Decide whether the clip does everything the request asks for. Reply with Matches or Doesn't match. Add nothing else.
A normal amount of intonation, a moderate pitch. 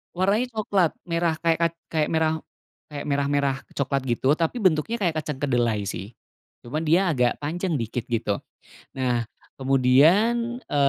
Matches